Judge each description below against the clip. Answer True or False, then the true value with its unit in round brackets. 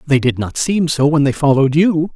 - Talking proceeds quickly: True (250 wpm)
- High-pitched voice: False (145 Hz)